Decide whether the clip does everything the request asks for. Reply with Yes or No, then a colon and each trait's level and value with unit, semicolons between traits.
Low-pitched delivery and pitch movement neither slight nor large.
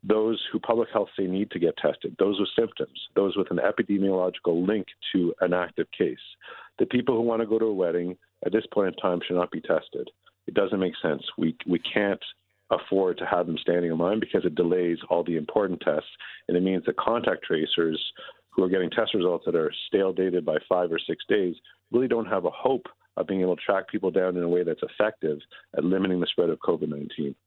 Yes: very low, 95 Hz; average, 3.3 semitones